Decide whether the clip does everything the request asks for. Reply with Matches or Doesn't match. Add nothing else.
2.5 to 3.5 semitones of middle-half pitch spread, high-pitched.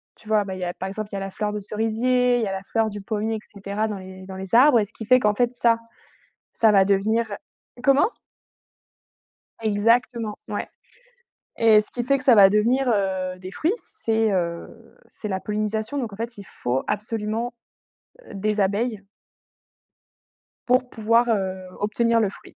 Matches